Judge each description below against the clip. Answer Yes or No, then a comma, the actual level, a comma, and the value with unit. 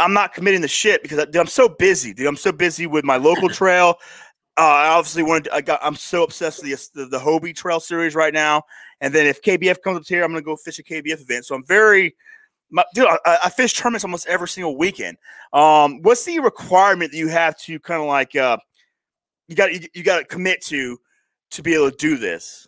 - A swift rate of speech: Yes, fast, 240 wpm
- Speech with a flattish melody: No, average, 3.4 semitones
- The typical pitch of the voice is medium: Yes, medium, 170 Hz